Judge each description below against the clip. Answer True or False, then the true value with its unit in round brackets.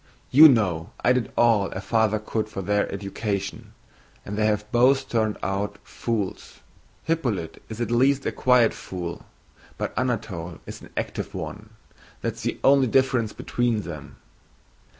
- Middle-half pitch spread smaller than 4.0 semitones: True (3.6 semitones)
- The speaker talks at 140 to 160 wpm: True (150 wpm)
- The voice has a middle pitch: False (110 Hz)